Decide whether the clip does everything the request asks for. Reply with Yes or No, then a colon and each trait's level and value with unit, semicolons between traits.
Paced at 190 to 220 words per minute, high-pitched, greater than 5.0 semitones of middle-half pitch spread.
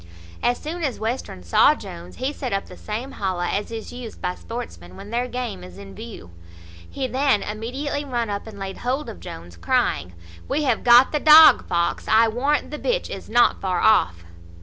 Yes: average, 195 wpm; high, 225 Hz; wide, 5.5 semitones